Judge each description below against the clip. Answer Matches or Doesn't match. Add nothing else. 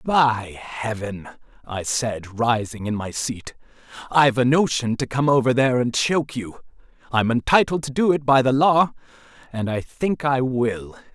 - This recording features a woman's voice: Doesn't match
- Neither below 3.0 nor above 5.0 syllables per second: Matches